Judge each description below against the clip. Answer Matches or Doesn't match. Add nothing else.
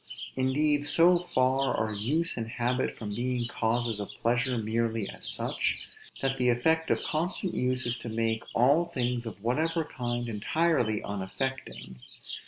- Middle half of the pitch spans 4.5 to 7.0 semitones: Doesn't match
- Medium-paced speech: Matches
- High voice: Doesn't match